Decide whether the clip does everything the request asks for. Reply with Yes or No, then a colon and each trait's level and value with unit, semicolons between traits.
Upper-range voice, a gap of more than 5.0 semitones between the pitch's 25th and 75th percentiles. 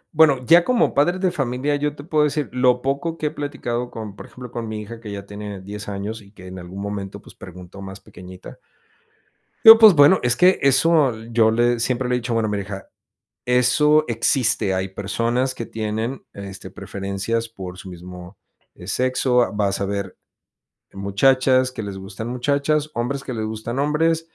No: low, 115 Hz; wide, 5.5 semitones